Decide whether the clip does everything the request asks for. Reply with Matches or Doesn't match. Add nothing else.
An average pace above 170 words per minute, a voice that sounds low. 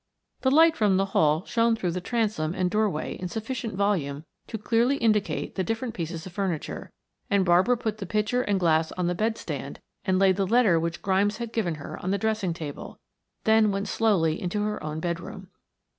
Doesn't match